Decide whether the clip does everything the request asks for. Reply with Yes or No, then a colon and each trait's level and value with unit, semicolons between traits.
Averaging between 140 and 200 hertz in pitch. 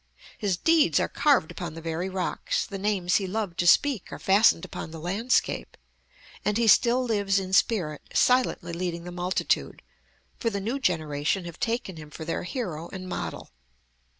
Yes: high, 190 Hz